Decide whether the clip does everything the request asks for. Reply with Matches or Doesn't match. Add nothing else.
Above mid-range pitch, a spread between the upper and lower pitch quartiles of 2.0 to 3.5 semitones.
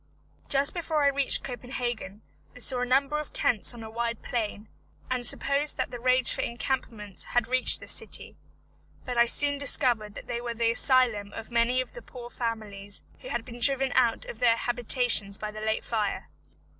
Matches